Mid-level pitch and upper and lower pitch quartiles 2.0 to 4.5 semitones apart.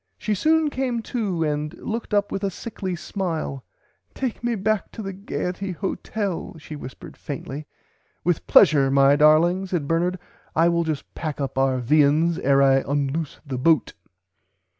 No: medium, 165 Hz; wide, 5.4 semitones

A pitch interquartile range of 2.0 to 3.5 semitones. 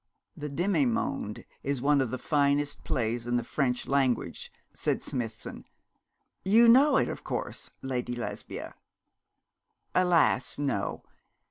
No: average, 4.9 semitones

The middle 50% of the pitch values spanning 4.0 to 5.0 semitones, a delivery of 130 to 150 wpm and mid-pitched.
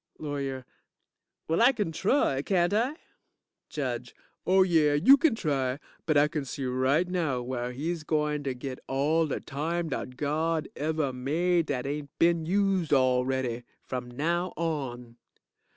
Yes: average, 4.4 semitones; average, 145 wpm; medium, 150 Hz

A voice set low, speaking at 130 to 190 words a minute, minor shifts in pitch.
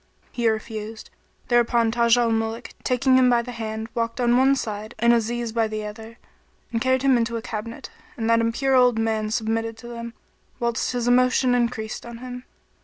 No: high, 235 Hz; average, 185 wpm; narrow, 1.6 semitones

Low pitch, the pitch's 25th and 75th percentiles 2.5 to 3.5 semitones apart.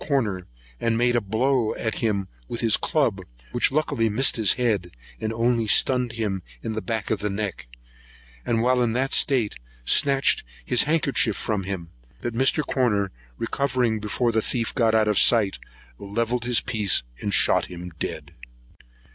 Yes: low, 115 Hz; average, 3.0 semitones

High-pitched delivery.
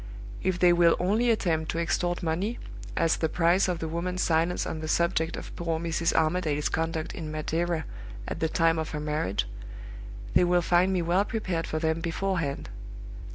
No: medium, 165 Hz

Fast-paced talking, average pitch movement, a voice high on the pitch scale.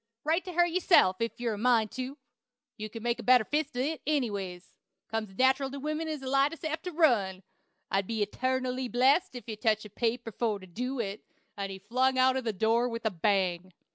Yes: fast, 220 wpm; average, 4.3 semitones; high, 245 Hz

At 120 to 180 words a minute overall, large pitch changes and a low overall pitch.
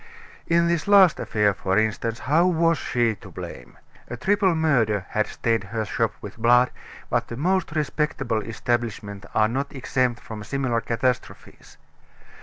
Yes: average, 150 wpm; wide, 6.1 semitones; low, 120 Hz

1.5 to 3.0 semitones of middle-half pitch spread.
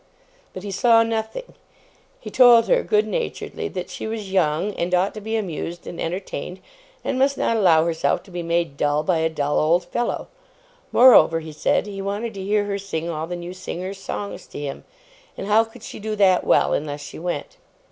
No: average, 4.8 semitones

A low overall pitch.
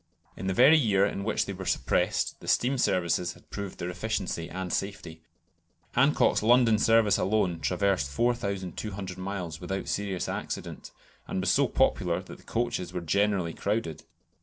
Yes: low, 100 Hz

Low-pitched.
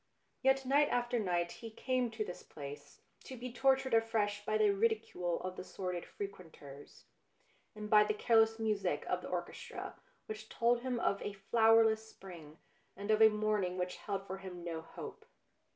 No: high, 215 Hz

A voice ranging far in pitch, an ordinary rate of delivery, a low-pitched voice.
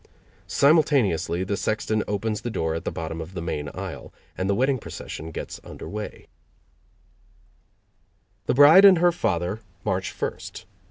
Yes: wide, 7.6 semitones; average, 150 wpm; low, 100 Hz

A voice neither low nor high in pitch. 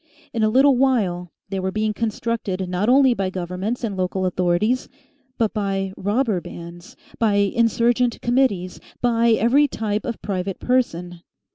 No: high, 210 Hz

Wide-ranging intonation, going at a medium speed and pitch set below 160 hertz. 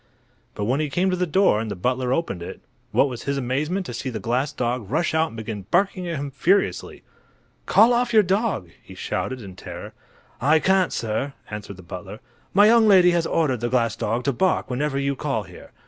No: wide, 7.3 semitones; fast, 215 wpm; medium, 140 Hz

